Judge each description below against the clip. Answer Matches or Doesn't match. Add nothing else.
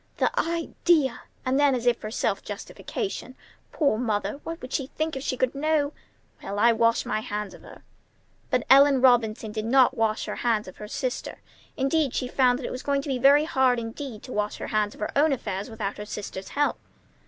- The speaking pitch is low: Doesn't match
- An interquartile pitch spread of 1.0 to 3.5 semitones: Doesn't match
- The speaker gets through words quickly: Matches